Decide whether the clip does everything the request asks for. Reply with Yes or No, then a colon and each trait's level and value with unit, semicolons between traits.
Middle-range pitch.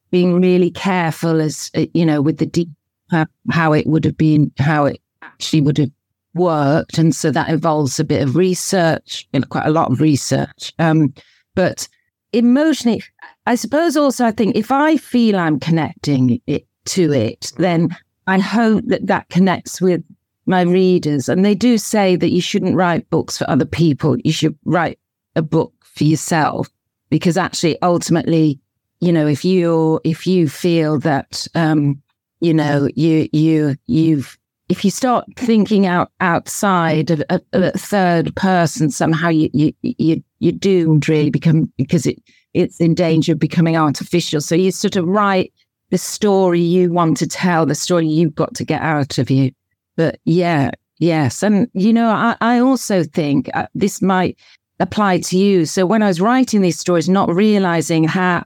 Yes: medium, 165 Hz